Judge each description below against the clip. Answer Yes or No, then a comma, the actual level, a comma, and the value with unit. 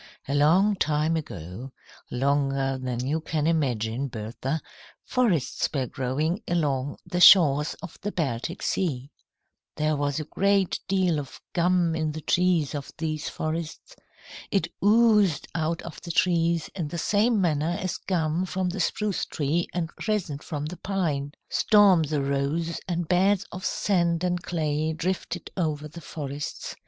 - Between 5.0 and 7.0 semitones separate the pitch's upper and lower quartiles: No, average, 3.8 semitones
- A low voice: No, medium, 160 Hz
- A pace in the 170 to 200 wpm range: No, average, 145 wpm